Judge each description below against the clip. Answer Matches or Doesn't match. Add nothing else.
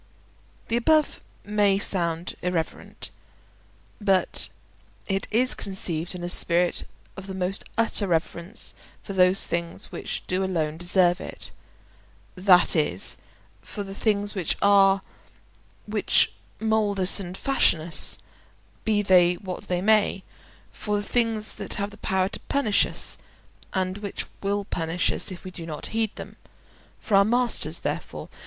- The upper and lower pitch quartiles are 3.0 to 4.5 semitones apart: Doesn't match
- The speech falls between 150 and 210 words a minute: Doesn't match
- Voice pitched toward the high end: Matches